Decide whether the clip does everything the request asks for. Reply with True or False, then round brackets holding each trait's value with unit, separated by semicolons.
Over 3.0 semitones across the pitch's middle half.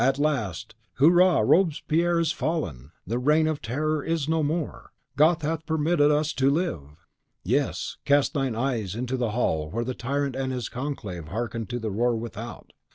True (5.0 semitones)